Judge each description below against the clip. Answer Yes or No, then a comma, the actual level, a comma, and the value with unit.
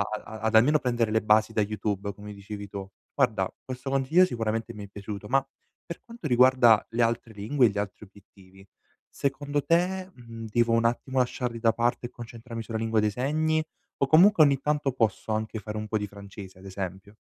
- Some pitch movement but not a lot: Yes, average, 4.0 semitones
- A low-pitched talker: Yes, low, 115 Hz